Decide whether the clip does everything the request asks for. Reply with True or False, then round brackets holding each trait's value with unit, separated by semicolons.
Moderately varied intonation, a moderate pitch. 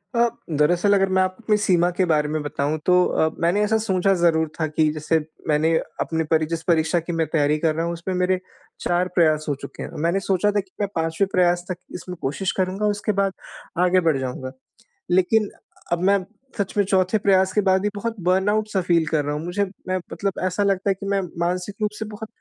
True (3.4 semitones; 180 Hz)